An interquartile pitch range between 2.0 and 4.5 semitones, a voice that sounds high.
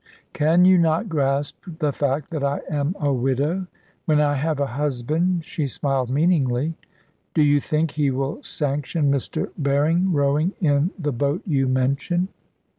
No: average, 2.9 semitones; medium, 145 Hz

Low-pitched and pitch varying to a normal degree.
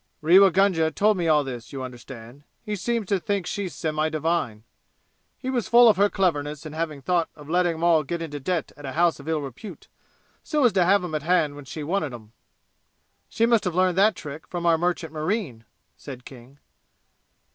No: medium, 165 Hz; average, 4.5 semitones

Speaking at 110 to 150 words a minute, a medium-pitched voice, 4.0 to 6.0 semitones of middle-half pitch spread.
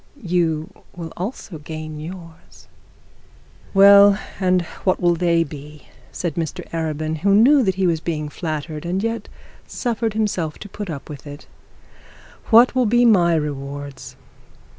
Yes: average, 140 wpm; medium, 170 Hz; average, 4.4 semitones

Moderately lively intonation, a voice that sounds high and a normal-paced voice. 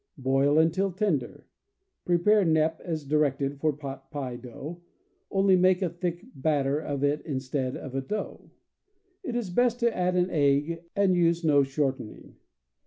No: average, 4.6 semitones; medium, 155 Hz; average, 160 wpm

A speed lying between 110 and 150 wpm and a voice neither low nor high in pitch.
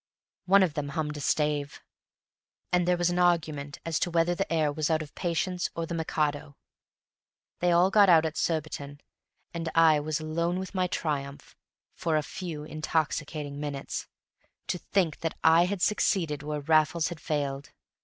No: average, 170 wpm; medium, 160 Hz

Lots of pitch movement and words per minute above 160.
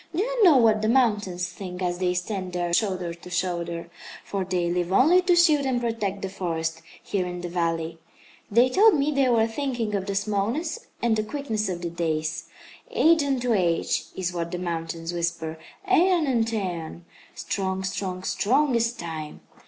Yes: wide, 5.8 semitones; average, 180 wpm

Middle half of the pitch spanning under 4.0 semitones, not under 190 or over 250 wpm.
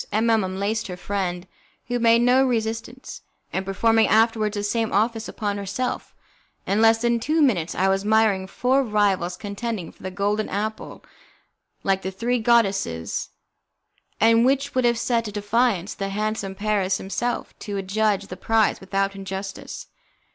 No: average, 2.8 semitones; average, 155 wpm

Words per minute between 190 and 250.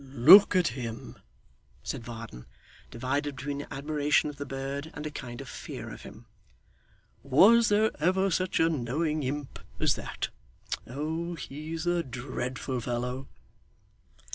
No: slow, 135 wpm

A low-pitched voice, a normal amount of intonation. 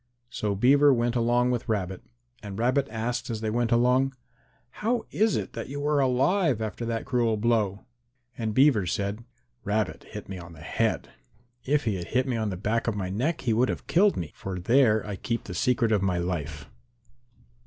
Yes: low, 115 Hz; average, 4.1 semitones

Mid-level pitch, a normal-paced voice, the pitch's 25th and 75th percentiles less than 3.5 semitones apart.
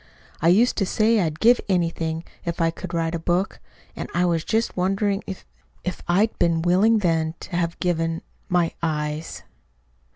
Yes: medium, 175 Hz; average, 170 wpm; average, 2.9 semitones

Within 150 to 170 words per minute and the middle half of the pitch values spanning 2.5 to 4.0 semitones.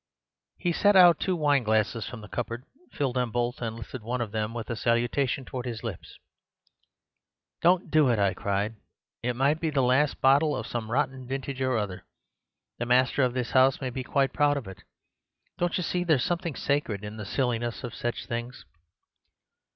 No: average, 190 wpm; average, 3.4 semitones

